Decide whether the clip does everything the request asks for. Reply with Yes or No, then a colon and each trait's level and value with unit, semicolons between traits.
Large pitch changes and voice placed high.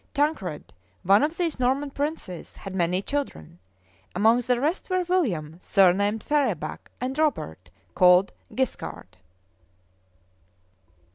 Yes: wide, 8.3 semitones; high, 230 Hz